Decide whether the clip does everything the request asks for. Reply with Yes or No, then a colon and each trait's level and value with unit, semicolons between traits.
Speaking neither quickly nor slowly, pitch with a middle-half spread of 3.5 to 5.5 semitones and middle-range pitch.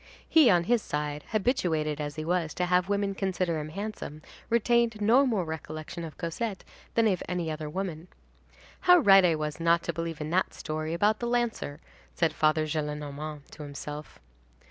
Yes: average, 175 wpm; average, 4.8 semitones; medium, 170 Hz